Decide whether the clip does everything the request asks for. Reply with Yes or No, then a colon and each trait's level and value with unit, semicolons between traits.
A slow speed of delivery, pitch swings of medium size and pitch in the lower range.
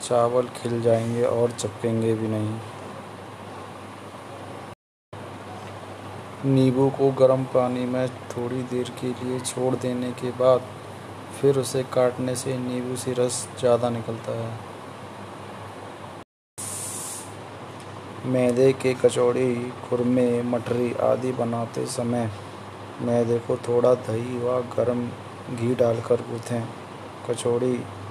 No: slow, 100 wpm; narrow, 2.0 semitones; low, 120 Hz